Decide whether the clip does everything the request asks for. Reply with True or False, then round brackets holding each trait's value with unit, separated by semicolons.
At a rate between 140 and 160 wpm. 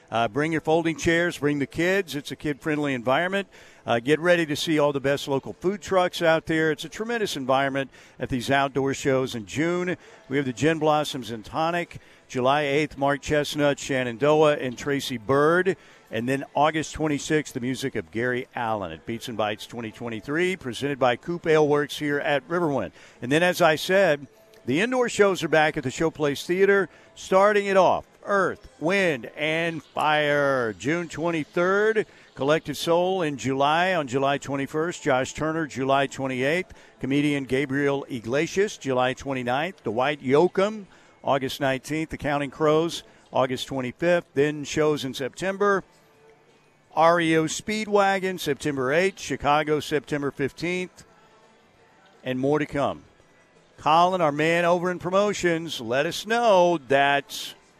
True (150 wpm)